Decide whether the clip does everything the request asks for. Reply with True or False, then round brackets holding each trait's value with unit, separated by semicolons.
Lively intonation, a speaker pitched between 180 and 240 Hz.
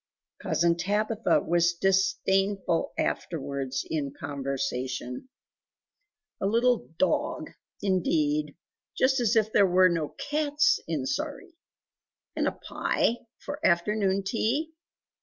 True (6.9 semitones; 190 Hz)